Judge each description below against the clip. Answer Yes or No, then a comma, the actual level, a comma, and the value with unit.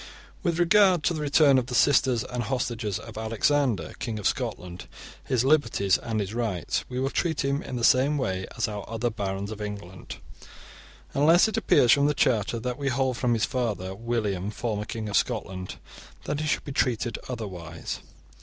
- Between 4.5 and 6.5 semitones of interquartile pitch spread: Yes, average, 4.9 semitones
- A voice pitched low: Yes, low, 120 Hz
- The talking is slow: No, average, 190 wpm